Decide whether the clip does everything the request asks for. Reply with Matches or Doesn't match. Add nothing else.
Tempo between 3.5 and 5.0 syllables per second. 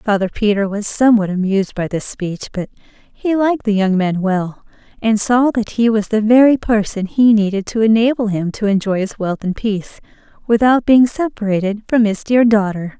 Doesn't match